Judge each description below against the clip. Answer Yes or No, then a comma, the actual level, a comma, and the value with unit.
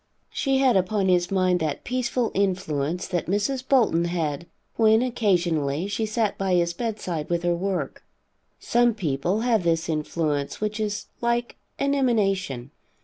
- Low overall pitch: No, high, 190 Hz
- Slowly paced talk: No, average, 145 wpm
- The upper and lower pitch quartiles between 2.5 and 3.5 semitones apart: No, average, 4.8 semitones